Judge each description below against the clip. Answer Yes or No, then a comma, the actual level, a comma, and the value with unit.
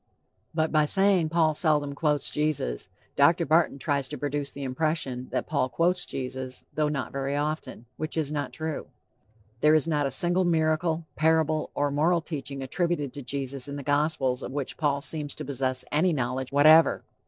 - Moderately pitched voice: Yes, medium, 150 Hz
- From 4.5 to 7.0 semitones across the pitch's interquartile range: No, narrow, 2.4 semitones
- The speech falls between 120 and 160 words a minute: No, average, 175 wpm